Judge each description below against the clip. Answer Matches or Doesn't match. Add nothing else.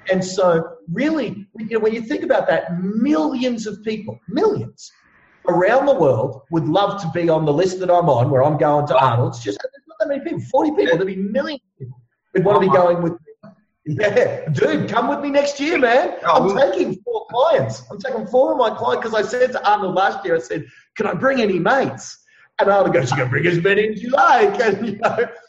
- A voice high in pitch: Matches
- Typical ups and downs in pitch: Doesn't match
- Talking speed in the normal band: Doesn't match